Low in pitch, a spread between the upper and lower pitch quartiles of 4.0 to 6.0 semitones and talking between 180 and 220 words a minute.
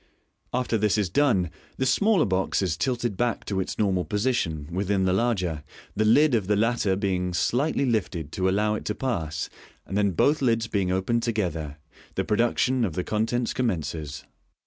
Yes: low, 105 Hz; average, 4.6 semitones; average, 195 wpm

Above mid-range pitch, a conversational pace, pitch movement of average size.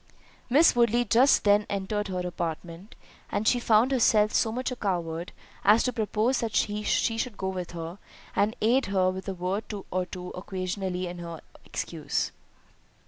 Yes: high, 200 Hz; average, 165 wpm; average, 3.8 semitones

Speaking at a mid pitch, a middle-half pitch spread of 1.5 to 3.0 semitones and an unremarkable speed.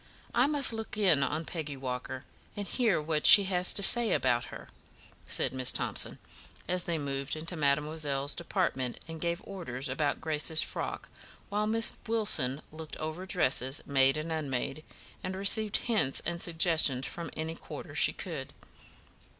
No: medium, 160 Hz; average, 5.2 semitones; average, 150 wpm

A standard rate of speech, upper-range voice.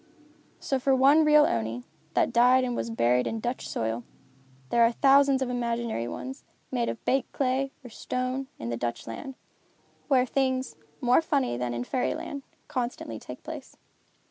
Yes: average, 170 wpm; very high, 250 Hz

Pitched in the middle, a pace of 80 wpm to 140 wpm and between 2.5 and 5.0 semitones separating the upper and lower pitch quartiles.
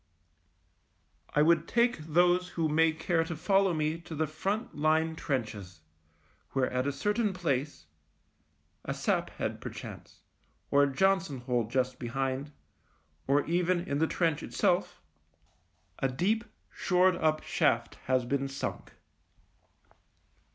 Yes: medium, 155 Hz; slow, 135 wpm; average, 4.6 semitones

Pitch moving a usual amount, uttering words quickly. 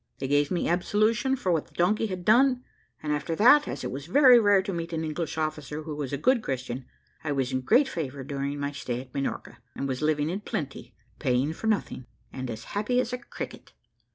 No: wide, 7.3 semitones; fast, 220 wpm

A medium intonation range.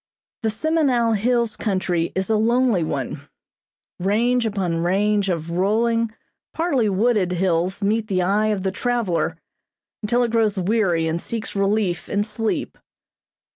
Yes: average, 3.8 semitones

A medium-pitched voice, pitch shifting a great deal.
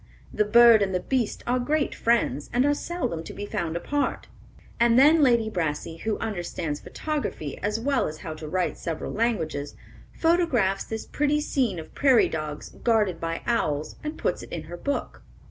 No: high, 220 Hz; wide, 7.8 semitones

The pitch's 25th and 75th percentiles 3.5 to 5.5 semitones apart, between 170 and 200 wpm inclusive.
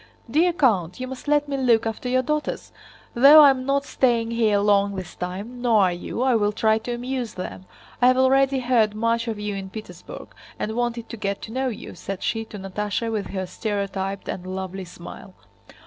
Yes: average, 4.4 semitones; average, 195 wpm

